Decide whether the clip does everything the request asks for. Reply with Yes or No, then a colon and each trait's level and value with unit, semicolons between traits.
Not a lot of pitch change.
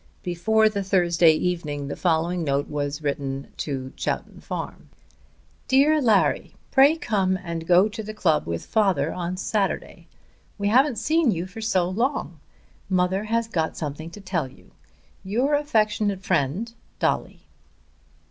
No: average, 5.2 semitones